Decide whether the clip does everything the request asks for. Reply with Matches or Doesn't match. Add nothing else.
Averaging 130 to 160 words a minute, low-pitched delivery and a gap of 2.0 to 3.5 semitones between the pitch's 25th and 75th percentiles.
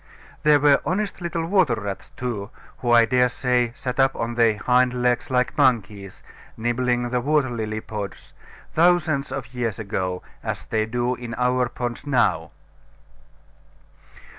Matches